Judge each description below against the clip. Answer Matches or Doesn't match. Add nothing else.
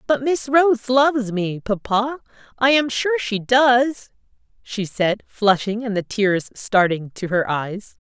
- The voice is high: Matches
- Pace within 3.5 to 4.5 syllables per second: Matches